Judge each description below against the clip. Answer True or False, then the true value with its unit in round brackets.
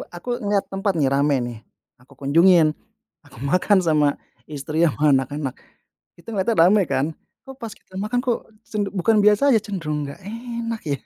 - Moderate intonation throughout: False (6.5 semitones)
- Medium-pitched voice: True (180 Hz)